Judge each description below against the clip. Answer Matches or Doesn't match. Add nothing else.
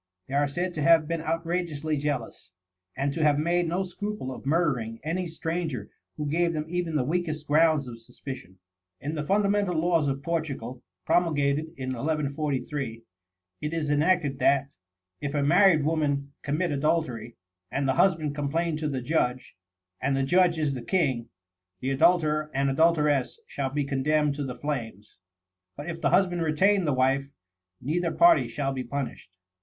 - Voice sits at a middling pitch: Matches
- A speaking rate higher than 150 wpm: Matches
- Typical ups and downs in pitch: Matches